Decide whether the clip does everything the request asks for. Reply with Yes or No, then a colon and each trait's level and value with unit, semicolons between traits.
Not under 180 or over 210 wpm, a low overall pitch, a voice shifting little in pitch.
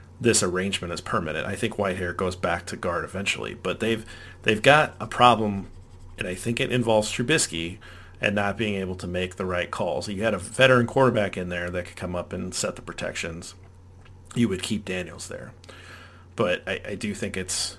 No: average, 200 wpm; very low, 95 Hz; average, 3.1 semitones